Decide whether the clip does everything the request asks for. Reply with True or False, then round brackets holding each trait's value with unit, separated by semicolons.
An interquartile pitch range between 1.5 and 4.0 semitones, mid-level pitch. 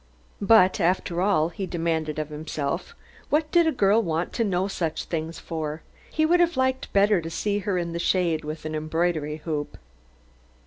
False (4.5 semitones; 175 Hz)